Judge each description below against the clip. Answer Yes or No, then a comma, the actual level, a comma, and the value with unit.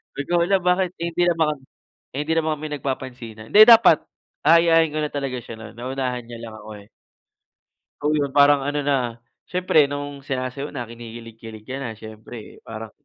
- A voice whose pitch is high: No, medium, 140 Hz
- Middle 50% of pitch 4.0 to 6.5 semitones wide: Yes, average, 4.7 semitones